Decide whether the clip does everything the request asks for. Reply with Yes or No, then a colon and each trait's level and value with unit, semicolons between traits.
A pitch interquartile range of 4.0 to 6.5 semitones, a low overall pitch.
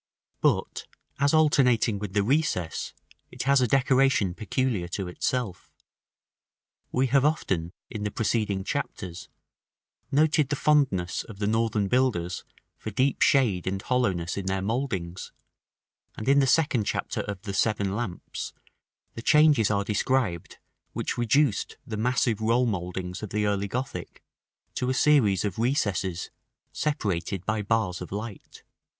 Yes: average, 5.2 semitones; low, 110 Hz